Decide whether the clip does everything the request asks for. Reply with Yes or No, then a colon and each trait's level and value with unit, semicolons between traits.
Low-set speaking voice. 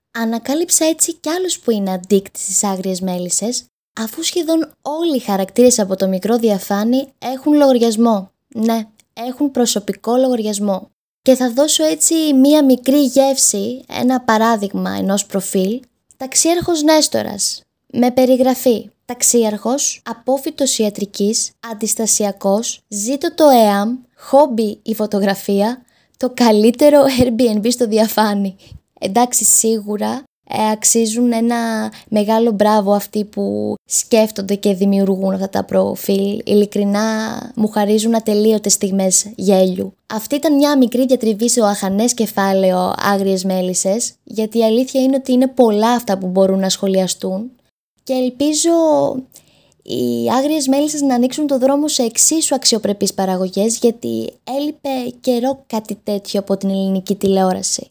No: high, 225 Hz